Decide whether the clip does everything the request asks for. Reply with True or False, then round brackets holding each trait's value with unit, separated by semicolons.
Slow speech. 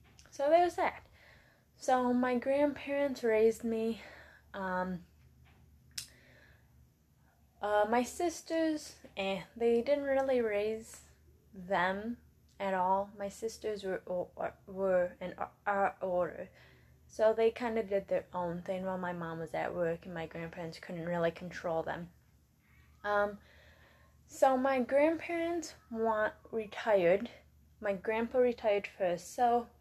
True (125 wpm)